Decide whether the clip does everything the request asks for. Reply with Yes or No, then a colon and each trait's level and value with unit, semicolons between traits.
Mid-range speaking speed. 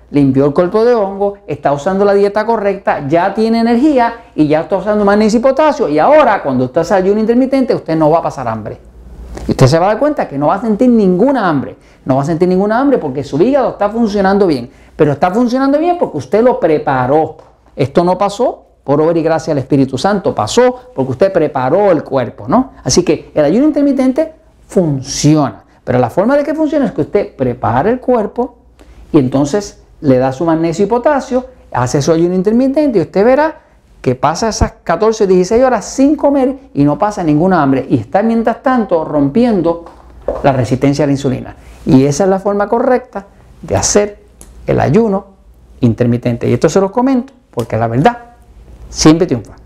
No: fast, 195 wpm